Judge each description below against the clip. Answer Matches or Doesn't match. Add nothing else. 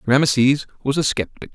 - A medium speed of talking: Matches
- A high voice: Doesn't match